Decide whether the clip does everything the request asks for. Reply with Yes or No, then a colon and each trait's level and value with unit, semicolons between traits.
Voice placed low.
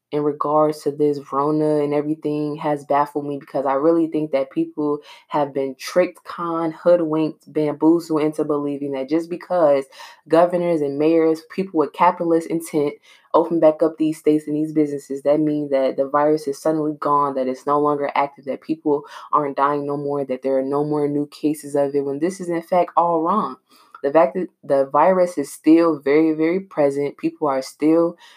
No: medium, 150 Hz